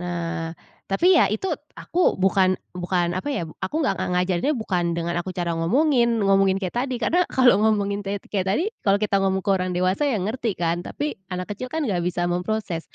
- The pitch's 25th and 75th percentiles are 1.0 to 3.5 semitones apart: No, average, 4.0 semitones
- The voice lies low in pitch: No, high, 195 Hz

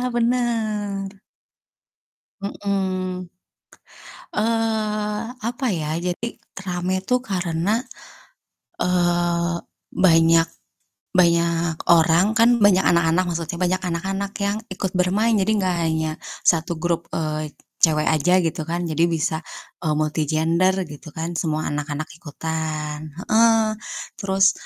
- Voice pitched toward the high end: No, medium, 175 Hz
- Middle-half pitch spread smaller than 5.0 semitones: Yes, average, 3.5 semitones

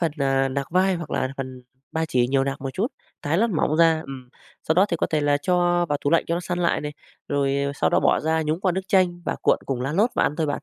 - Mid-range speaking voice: Yes, medium, 160 Hz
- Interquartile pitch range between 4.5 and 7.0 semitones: No, average, 4.1 semitones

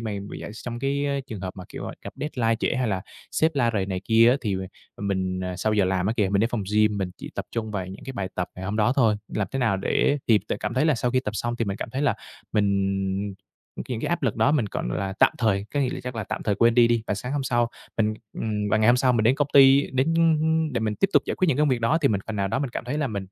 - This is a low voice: Yes, low, 115 Hz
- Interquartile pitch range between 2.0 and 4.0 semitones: No, average, 4.8 semitones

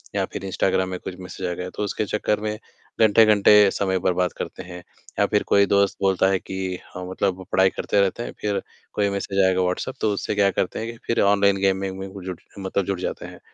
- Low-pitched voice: Yes, very low, 95 Hz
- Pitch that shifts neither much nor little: No, narrow, 1.5 semitones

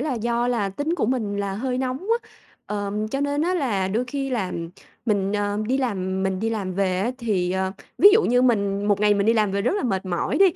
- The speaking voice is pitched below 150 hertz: No, high, 210 Hz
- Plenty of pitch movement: No, average, 4.3 semitones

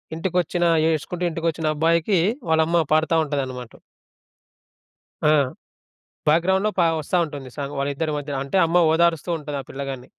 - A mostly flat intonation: No, average, 3.0 semitones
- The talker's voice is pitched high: No, medium, 160 Hz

